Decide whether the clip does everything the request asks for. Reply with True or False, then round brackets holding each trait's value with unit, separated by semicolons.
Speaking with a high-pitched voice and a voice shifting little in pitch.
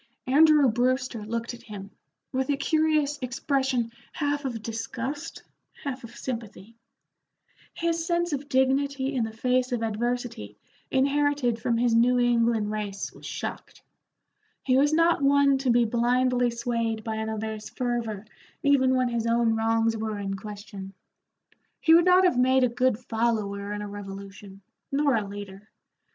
False (240 Hz; 3.6 semitones)